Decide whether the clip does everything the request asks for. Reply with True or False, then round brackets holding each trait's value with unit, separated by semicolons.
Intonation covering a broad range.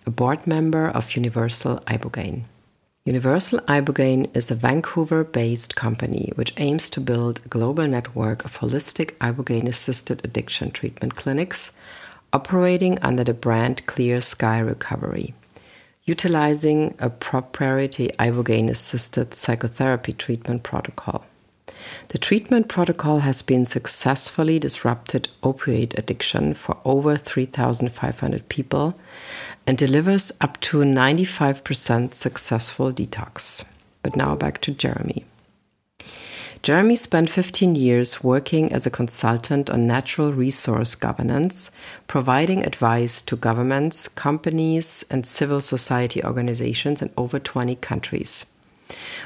False (4.1 semitones)